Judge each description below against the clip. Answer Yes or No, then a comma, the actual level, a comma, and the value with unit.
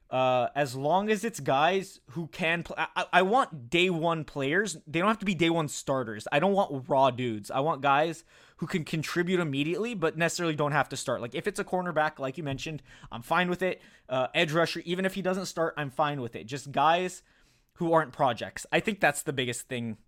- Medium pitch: Yes, medium, 160 Hz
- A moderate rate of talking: No, fast, 225 wpm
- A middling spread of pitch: Yes, average, 4.5 semitones